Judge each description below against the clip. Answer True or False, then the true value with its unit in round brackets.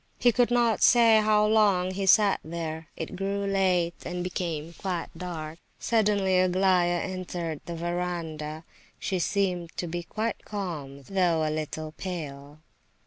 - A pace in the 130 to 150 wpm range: True (140 wpm)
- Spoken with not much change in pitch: False (3.3 semitones)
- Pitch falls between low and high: True (180 Hz)